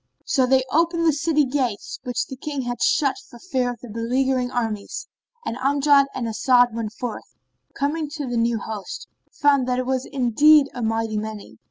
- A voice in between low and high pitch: No, very high, 255 Hz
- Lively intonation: No, average, 3.5 semitones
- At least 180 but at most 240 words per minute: Yes, average, 190 wpm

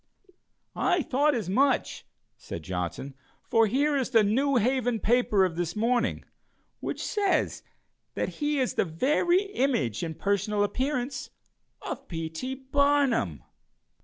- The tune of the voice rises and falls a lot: Yes, wide, 6.6 semitones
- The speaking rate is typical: No, slow, 130 wpm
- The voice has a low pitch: No, high, 245 Hz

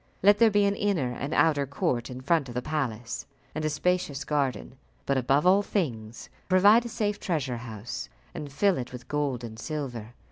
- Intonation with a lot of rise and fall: Yes, wide, 6.7 semitones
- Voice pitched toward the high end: No, medium, 145 Hz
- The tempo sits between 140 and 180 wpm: No, average, 190 wpm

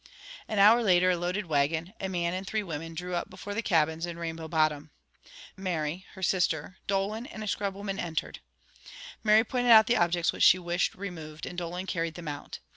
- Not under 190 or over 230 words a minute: Yes, average, 195 wpm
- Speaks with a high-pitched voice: No, medium, 180 Hz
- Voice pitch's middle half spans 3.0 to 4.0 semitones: Yes, average, 3.3 semitones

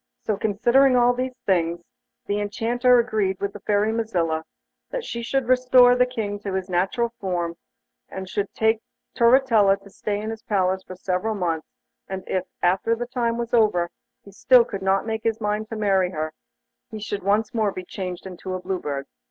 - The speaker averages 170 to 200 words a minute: Yes, average, 195 wpm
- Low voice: No, high, 205 Hz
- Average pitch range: Yes, average, 3.7 semitones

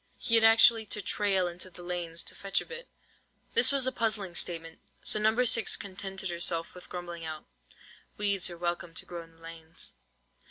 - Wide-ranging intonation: No, average, 3.9 semitones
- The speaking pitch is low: No, medium, 185 Hz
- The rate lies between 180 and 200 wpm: Yes, average, 190 wpm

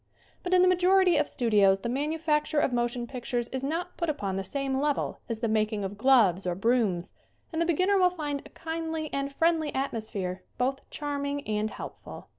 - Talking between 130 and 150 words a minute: No, average, 195 wpm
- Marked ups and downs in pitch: Yes, wide, 6.5 semitones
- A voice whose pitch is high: Yes, very high, 275 Hz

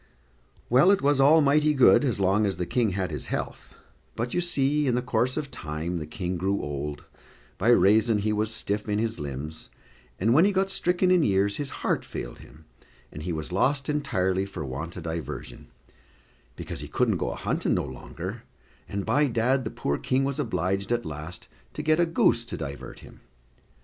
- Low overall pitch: Yes, low, 110 Hz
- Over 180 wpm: Yes, average, 200 wpm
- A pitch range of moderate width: No, wide, 7.7 semitones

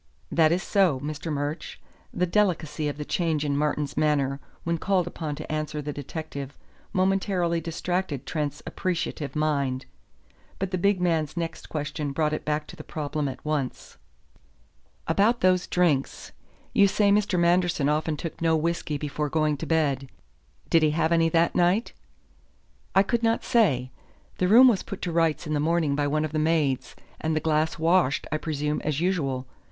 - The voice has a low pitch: No, medium, 155 Hz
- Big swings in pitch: No, average, 3.1 semitones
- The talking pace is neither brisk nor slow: Yes, average, 175 wpm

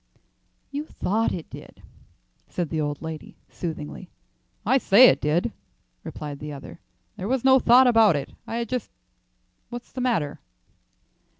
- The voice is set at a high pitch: Yes, high, 195 Hz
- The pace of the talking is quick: No, average, 145 wpm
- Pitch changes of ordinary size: No, wide, 8.5 semitones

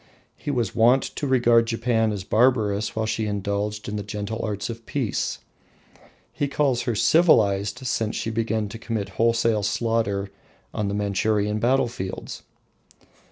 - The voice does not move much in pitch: Yes, narrow, 2.3 semitones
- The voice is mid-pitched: No, low, 110 Hz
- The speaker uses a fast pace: No, average, 140 wpm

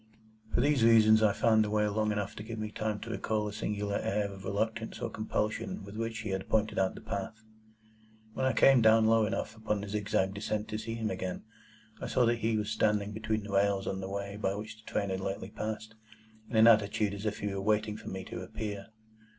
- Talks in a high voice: No, low, 105 Hz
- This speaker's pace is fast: Yes, fast, 230 wpm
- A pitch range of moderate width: No, narrow, 1.6 semitones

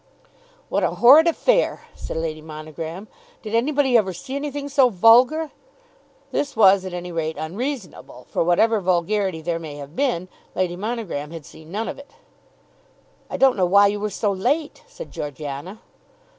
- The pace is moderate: Yes, average, 160 wpm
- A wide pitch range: Yes, wide, 7.3 semitones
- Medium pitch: No, high, 195 Hz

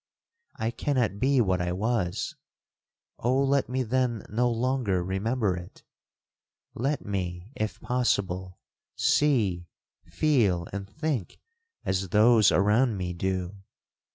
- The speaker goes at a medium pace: No, slow, 110 wpm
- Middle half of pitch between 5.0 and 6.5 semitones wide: Yes, average, 5.3 semitones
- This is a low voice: Yes, low, 105 Hz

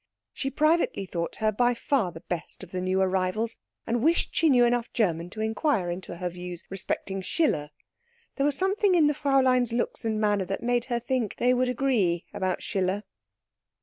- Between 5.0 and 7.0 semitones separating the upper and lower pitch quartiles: Yes, wide, 5.6 semitones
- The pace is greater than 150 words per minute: Yes, average, 185 wpm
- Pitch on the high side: Yes, high, 220 Hz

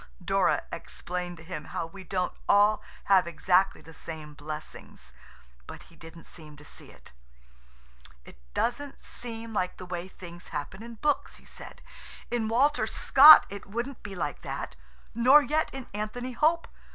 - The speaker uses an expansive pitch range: Yes, wide, 6.0 semitones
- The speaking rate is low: No, average, 160 wpm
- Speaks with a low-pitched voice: No, high, 195 Hz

